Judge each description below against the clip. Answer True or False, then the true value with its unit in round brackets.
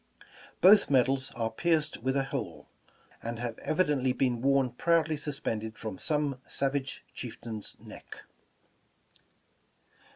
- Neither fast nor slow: False (120 wpm)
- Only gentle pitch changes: False (3.8 semitones)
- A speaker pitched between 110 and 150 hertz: True (135 Hz)